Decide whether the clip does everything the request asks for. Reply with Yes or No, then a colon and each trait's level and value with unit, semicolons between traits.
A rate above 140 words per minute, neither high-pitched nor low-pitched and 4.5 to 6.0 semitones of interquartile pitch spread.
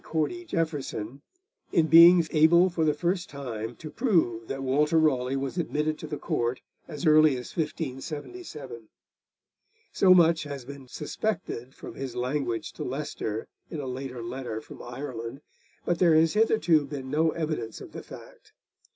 No: average, 155 wpm; medium, 150 Hz; average, 4.1 semitones